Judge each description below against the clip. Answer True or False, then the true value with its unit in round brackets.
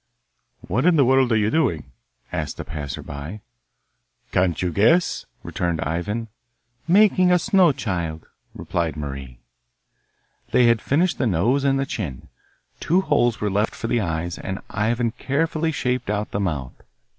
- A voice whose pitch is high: False (110 Hz)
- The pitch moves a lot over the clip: True (8.3 semitones)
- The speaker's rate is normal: True (155 wpm)